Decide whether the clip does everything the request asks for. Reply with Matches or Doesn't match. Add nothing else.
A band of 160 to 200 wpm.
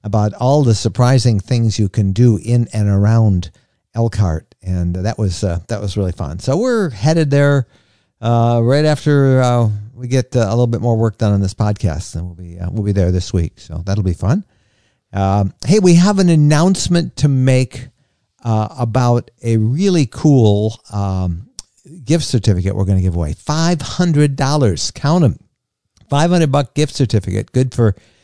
Matches